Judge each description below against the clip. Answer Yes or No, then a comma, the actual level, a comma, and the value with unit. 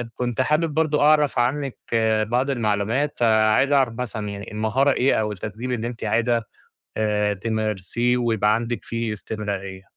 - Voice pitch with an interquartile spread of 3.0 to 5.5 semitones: Yes, average, 3.3 semitones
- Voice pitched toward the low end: Yes, low, 115 Hz